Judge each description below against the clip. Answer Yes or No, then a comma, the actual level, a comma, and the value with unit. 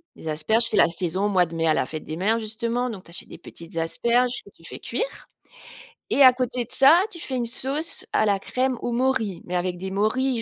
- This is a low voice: No, high, 220 Hz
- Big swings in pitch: Yes, wide, 5.9 semitones